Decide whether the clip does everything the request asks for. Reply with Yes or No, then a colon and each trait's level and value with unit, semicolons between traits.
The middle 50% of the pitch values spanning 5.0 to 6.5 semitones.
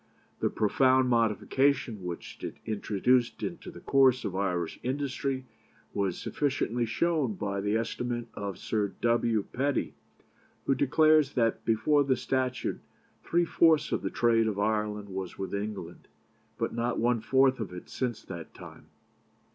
No: average, 4.3 semitones